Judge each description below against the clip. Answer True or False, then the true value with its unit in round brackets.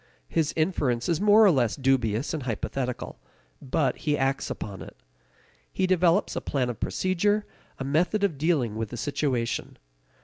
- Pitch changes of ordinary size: False (5.9 semitones)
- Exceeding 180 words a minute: False (160 wpm)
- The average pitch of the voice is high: False (140 Hz)